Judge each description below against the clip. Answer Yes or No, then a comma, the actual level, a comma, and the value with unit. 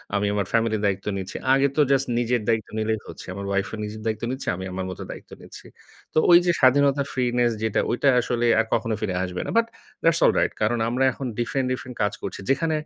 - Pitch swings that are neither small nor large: Yes, average, 4.2 semitones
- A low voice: Yes, low, 120 Hz